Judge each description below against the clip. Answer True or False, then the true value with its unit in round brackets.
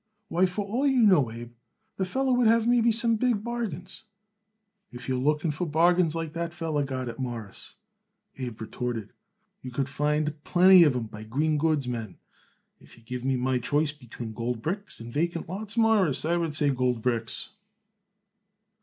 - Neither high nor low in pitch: True (150 Hz)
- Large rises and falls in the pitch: True (6.9 semitones)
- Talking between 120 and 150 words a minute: False (180 wpm)